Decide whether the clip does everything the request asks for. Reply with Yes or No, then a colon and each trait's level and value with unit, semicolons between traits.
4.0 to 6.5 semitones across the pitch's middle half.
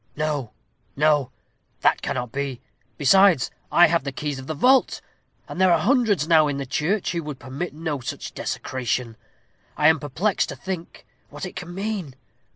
Yes: average, 4.5 semitones